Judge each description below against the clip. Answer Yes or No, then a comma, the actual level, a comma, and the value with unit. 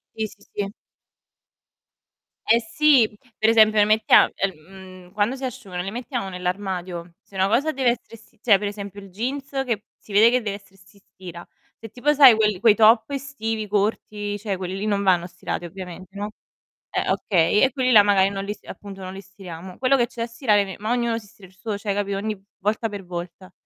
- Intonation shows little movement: No, average, 3.0 semitones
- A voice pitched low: No, high, 205 Hz